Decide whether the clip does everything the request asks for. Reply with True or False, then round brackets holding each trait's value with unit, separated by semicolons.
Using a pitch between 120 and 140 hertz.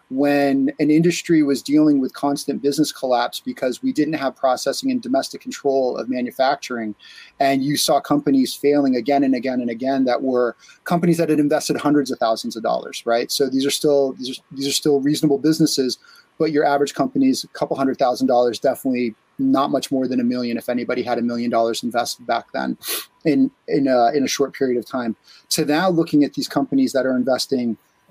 True (135 Hz)